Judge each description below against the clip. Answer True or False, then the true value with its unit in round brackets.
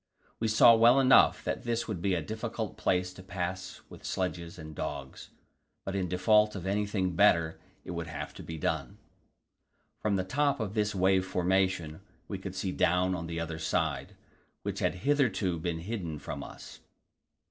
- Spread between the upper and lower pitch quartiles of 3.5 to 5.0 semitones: True (3.9 semitones)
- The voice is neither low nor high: False (95 Hz)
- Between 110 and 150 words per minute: False (175 wpm)